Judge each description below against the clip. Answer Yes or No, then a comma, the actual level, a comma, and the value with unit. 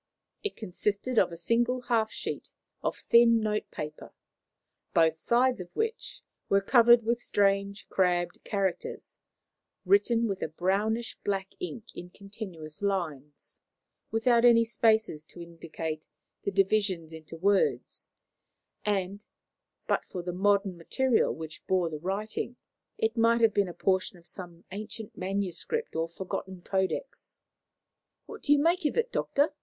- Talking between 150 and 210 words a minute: No, average, 140 wpm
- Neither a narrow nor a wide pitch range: Yes, average, 4.7 semitones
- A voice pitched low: No, high, 200 Hz